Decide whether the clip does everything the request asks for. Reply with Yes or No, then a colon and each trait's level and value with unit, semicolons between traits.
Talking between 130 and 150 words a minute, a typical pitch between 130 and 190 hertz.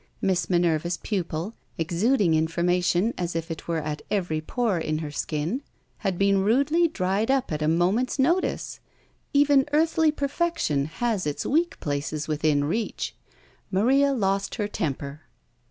Yes: average, 140 wpm; medium, 185 Hz